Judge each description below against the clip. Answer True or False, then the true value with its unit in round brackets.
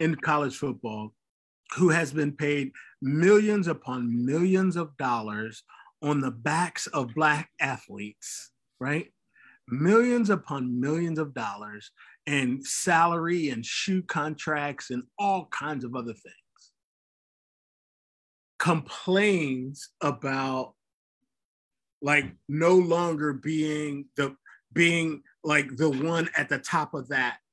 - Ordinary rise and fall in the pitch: True (3.9 semitones)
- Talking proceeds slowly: True (110 wpm)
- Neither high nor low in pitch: True (150 Hz)